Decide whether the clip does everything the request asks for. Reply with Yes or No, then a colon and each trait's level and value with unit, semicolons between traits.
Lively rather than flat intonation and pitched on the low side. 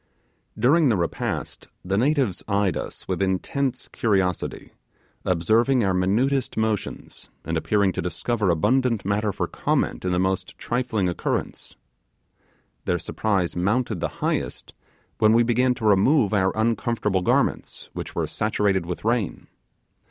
No: average, 4.0 semitones; low, 105 Hz